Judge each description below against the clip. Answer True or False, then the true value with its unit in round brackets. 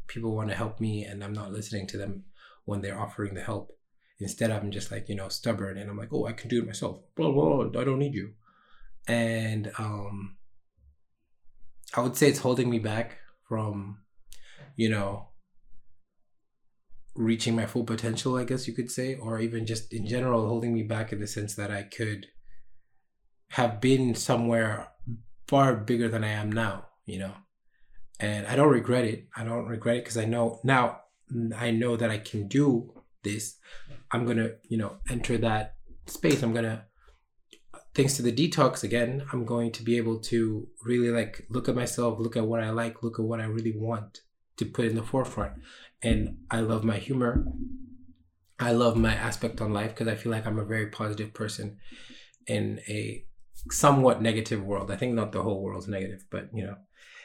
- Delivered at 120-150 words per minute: False (190 wpm)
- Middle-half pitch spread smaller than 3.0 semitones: True (2.4 semitones)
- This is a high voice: False (115 Hz)